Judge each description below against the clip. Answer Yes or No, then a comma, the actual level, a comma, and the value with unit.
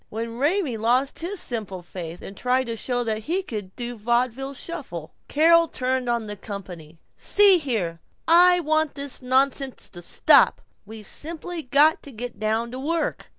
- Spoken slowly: No, average, 170 wpm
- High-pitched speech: Yes, very high, 250 Hz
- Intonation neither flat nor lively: No, wide, 5.9 semitones